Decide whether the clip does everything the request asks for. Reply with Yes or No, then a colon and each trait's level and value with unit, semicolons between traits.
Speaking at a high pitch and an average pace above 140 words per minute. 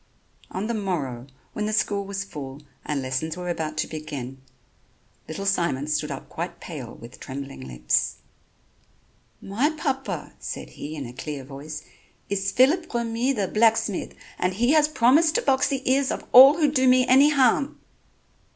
Yes: high, 195 Hz; average, 165 wpm